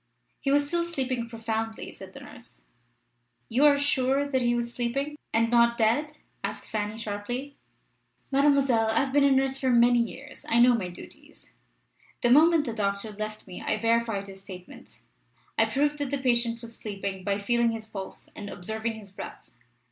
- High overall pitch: Yes, high, 235 Hz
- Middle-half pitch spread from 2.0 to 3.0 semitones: No, average, 3.7 semitones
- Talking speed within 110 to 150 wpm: No, average, 180 wpm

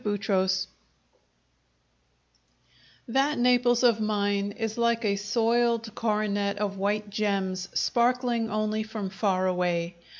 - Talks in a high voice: Yes, high, 210 Hz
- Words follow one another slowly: Yes, slow, 110 wpm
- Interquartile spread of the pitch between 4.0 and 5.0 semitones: No, average, 2.7 semitones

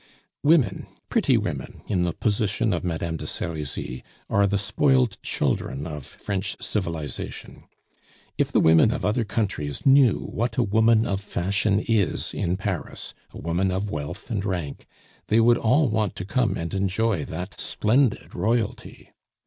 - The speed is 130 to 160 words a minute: Yes, average, 150 wpm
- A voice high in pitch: No, low, 100 Hz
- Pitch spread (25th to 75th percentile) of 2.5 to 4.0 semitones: No, average, 4.5 semitones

